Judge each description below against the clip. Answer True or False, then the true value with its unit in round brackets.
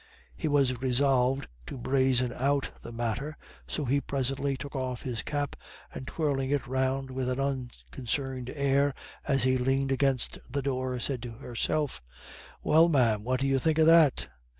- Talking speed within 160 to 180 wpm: True (165 wpm)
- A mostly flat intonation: True (1.7 semitones)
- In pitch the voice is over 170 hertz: False (135 Hz)